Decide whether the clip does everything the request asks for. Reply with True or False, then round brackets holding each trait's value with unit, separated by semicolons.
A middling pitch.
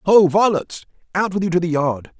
True (175 Hz)